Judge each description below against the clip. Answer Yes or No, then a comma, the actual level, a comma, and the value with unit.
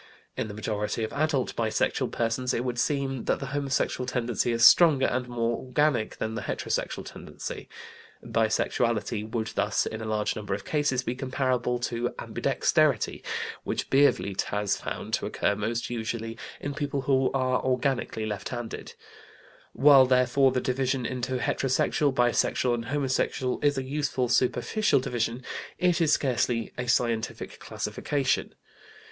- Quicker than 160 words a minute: No, average, 145 wpm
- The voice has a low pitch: Yes, low, 125 Hz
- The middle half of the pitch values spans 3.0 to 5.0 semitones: No, narrow, 2.5 semitones